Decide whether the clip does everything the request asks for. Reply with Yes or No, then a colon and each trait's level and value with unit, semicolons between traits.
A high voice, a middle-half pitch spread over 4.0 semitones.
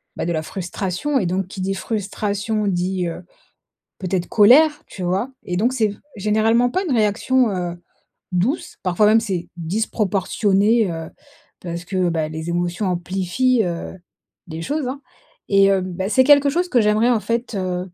Yes: high, 195 Hz; average, 4.4 semitones